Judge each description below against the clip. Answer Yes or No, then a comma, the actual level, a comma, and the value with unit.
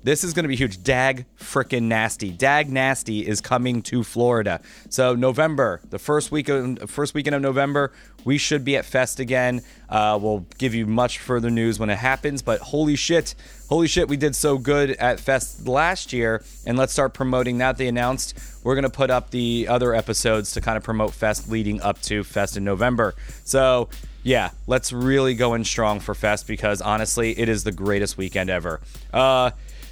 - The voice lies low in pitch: Yes, low, 125 Hz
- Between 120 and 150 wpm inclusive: No, average, 200 wpm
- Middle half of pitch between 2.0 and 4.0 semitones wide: Yes, average, 3.6 semitones